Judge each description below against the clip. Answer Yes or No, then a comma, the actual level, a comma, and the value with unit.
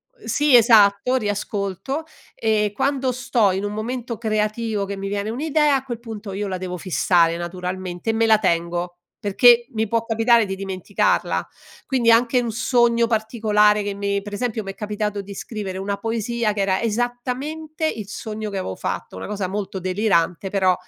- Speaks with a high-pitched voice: Yes, high, 210 Hz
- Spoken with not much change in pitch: No, average, 3.2 semitones